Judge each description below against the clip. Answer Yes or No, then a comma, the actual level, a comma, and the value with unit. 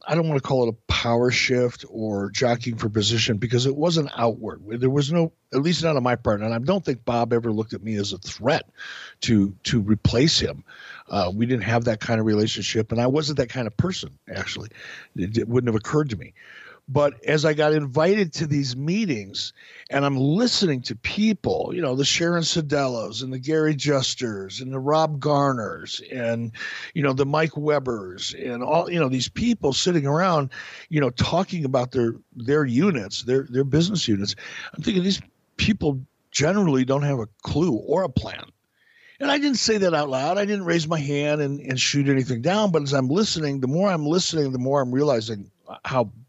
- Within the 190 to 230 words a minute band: Yes, fast, 205 wpm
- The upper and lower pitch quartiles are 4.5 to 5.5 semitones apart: Yes, average, 4.9 semitones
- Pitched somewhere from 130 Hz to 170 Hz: Yes, low, 135 Hz